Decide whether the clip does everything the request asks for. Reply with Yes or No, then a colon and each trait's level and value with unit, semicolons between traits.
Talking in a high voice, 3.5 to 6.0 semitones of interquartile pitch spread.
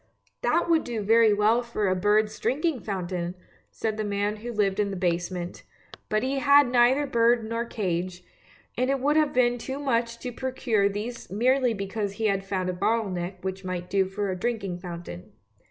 Yes: high, 215 Hz; average, 4.1 semitones